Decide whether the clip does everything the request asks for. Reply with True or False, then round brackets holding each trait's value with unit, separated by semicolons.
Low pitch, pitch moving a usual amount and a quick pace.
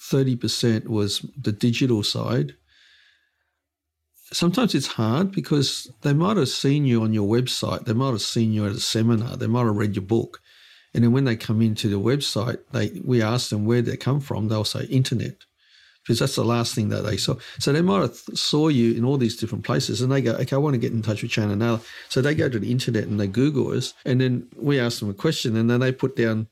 True (120 Hz; 3.4 semitones; 240 wpm)